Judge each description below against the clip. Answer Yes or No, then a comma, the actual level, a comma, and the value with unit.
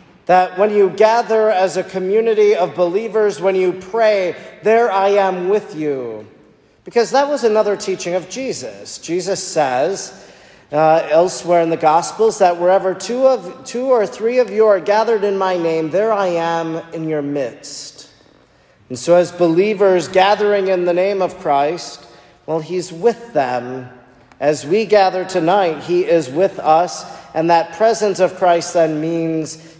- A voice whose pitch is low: No, medium, 185 Hz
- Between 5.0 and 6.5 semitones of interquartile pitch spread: No, average, 3.9 semitones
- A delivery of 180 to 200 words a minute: No, average, 160 wpm